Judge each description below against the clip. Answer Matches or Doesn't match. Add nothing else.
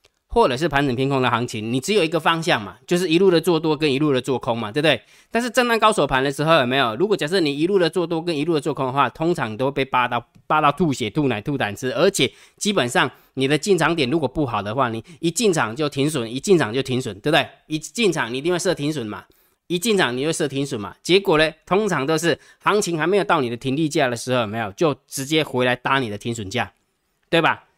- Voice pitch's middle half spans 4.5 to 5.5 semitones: Matches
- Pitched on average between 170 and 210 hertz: Doesn't match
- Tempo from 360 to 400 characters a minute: Matches